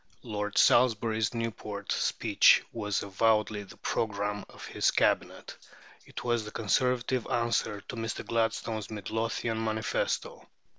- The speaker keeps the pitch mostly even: Yes, narrow, 1.8 semitones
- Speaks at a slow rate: Yes, slow, 115 wpm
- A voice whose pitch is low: Yes, low, 110 Hz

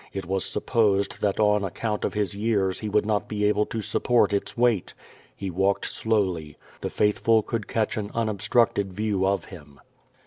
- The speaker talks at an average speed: Yes, average, 175 wpm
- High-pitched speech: No, low, 105 Hz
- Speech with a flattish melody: Yes, narrow, 2.0 semitones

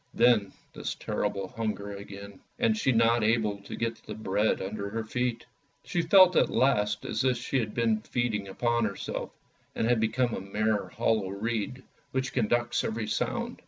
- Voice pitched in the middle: No, low, 110 Hz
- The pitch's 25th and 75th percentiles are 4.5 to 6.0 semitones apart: No, average, 2.8 semitones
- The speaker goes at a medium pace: Yes, average, 175 wpm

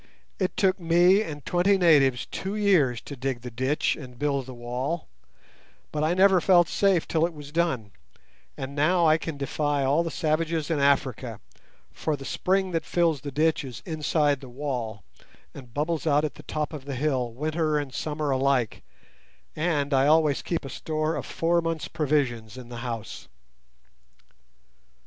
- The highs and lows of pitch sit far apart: No, average, 3.7 semitones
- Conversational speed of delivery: Yes, average, 170 wpm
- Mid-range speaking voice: Yes, medium, 150 Hz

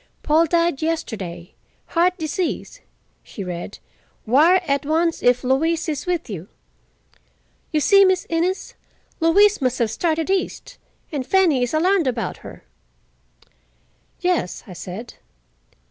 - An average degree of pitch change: No, wide, 5.9 semitones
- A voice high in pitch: Yes, very high, 315 Hz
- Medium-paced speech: No, slow, 125 wpm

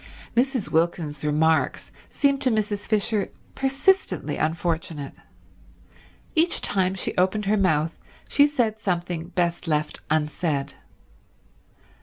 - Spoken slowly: Yes, slow, 105 wpm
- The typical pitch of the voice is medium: Yes, medium, 180 Hz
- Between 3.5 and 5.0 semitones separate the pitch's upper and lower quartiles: No, wide, 5.5 semitones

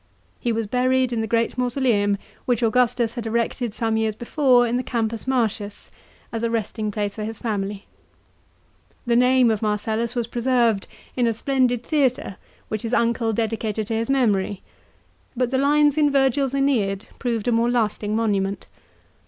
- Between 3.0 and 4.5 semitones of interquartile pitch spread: No, narrow, 2.4 semitones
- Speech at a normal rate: Yes, average, 165 wpm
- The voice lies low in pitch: No, high, 230 Hz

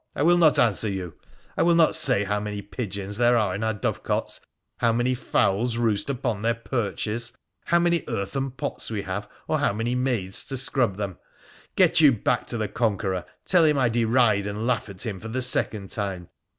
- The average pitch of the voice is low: Yes, low, 115 Hz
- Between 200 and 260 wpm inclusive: Yes, fast, 205 wpm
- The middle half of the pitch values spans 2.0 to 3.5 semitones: No, average, 3.9 semitones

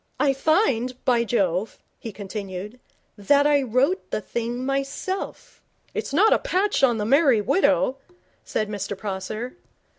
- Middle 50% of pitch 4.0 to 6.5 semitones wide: Yes, average, 5.2 semitones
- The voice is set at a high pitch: Yes, very high, 250 Hz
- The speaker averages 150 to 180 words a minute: No, average, 140 wpm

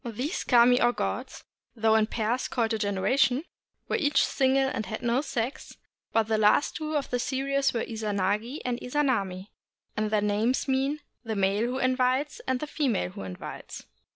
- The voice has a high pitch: Yes, high, 240 Hz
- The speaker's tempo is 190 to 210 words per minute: No, average, 180 wpm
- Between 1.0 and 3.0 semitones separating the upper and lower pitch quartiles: No, average, 3.8 semitones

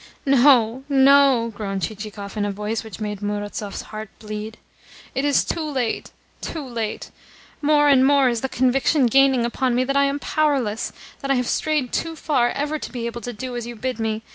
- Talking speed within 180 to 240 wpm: Yes, average, 195 wpm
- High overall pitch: Yes, high, 245 Hz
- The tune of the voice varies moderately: Yes, average, 4.1 semitones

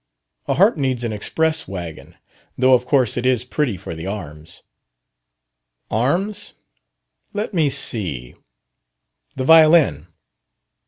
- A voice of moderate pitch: No, low, 125 Hz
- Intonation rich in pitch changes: Yes, wide, 8.7 semitones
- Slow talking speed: Yes, slow, 115 wpm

